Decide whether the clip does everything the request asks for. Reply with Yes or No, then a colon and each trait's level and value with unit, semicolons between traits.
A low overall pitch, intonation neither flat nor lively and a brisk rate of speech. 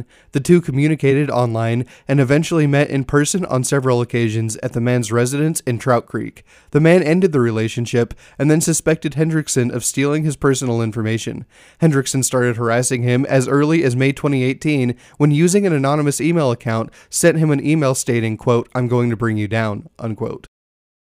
No: low, 130 Hz; average, 3.7 semitones; average, 175 wpm